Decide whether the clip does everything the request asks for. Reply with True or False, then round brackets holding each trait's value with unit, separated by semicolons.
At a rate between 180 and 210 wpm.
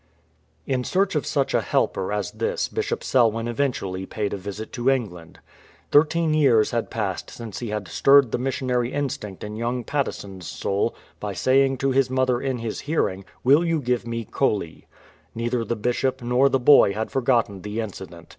True (185 wpm)